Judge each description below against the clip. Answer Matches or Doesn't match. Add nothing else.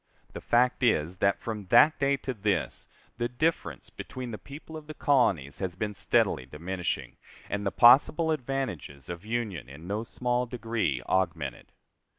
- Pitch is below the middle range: Matches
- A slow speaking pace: Doesn't match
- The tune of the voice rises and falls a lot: Matches